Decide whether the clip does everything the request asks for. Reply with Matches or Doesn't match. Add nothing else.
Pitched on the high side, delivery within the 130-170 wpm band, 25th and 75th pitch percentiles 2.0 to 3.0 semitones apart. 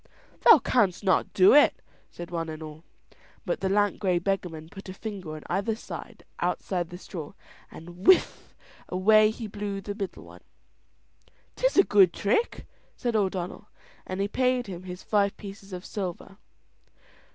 Matches